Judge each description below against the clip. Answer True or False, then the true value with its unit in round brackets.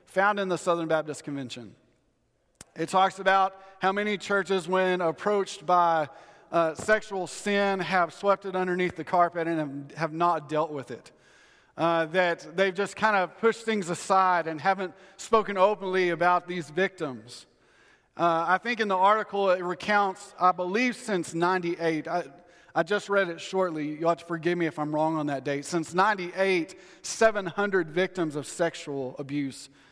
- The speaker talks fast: False (165 wpm)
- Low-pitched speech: False (180 Hz)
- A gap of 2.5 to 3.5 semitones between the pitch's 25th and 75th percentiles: True (3.0 semitones)